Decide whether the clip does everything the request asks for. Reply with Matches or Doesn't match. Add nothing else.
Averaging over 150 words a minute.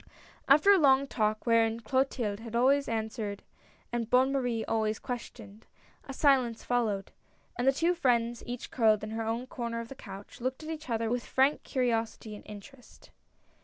Matches